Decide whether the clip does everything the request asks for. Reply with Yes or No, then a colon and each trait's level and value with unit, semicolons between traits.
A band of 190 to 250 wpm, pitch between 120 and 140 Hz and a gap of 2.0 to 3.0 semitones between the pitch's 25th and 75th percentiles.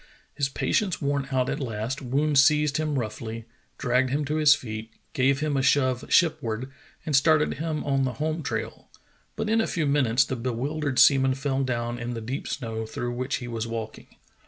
No: average, 195 wpm; low, 135 Hz; average, 3.5 semitones